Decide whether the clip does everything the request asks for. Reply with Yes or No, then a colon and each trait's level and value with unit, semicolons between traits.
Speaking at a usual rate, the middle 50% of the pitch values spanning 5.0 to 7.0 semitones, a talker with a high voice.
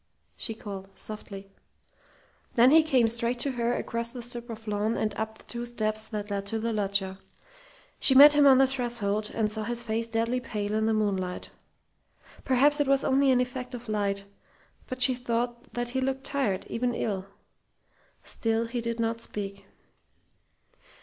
No: average, 175 wpm; average, 2.7 semitones; high, 230 Hz